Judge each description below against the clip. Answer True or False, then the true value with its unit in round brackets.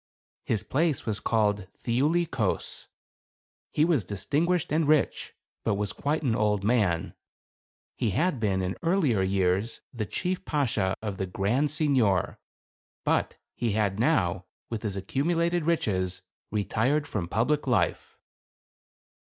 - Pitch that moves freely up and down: True (7.3 semitones)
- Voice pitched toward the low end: True (110 Hz)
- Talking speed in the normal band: False (130 wpm)